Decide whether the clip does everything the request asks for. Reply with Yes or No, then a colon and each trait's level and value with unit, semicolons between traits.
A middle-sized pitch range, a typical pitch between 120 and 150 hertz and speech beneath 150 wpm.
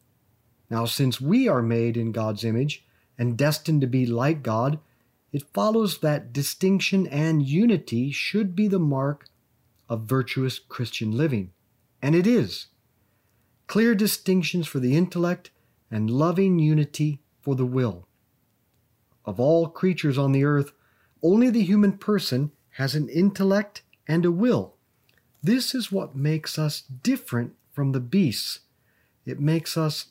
No: wide, 6.2 semitones; medium, 140 Hz; average, 140 wpm